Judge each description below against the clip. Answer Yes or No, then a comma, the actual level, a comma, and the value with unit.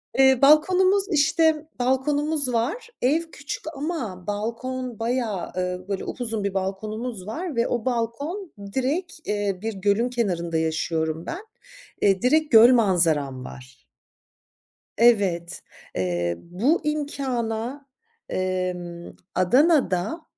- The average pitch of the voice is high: Yes, high, 230 Hz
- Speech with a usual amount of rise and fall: No, wide, 7.4 semitones